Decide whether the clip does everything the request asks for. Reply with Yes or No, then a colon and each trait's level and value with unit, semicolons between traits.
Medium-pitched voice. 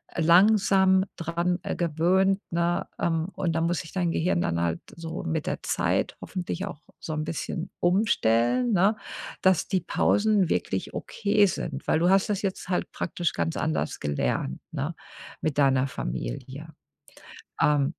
Yes: medium, 170 Hz